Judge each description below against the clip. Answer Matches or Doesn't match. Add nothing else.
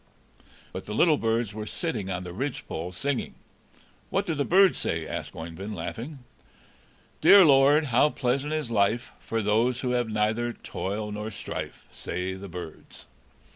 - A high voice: Doesn't match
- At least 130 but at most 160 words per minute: Matches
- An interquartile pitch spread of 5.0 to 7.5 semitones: Matches